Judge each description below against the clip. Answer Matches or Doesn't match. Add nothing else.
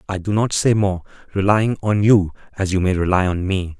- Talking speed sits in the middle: Doesn't match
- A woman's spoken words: Doesn't match